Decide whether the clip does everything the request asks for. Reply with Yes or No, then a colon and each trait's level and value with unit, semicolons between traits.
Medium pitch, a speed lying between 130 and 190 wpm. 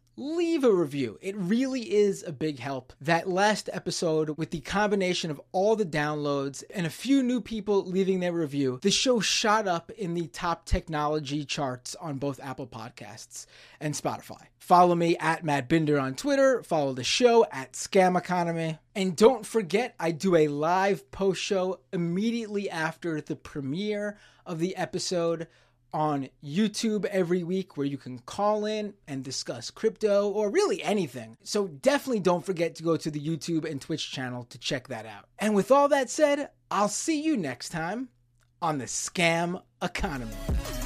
Yes: medium, 175 Hz; average, 170 wpm